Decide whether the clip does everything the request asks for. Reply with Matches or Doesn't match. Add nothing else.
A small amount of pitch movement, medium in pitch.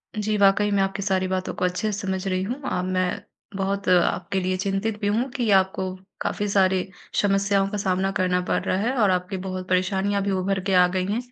Doesn't match